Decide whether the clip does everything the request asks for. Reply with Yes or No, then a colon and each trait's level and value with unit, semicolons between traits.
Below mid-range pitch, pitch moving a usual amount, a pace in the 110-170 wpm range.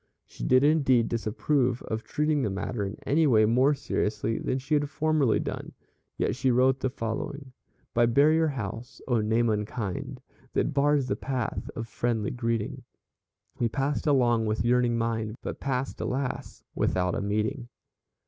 Yes: low, 125 Hz; average, 3.6 semitones; average, 160 wpm